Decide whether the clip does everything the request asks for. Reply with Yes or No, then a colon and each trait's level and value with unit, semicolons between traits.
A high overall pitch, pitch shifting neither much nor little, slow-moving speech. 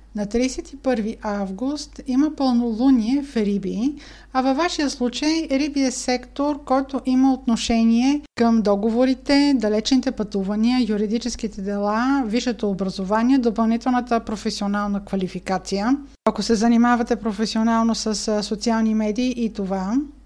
Yes: high, 235 Hz; average, 3.4 semitones; slow, 110 wpm